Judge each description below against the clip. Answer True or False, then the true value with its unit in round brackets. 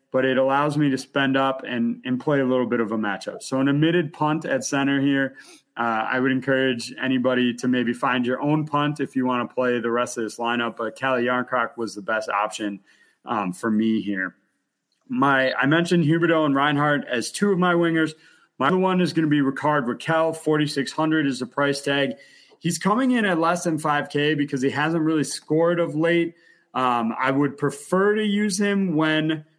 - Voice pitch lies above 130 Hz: True (140 Hz)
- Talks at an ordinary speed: False (215 wpm)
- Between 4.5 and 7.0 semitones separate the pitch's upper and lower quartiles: False (3.8 semitones)